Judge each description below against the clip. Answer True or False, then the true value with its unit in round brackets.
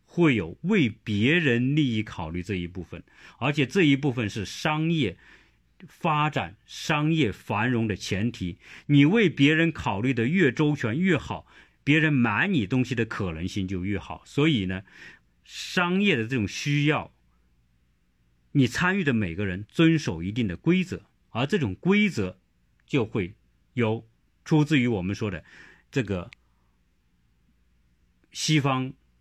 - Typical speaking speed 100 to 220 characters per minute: True (205 characters per minute)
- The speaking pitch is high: False (115 Hz)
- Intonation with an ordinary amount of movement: False (8.9 semitones)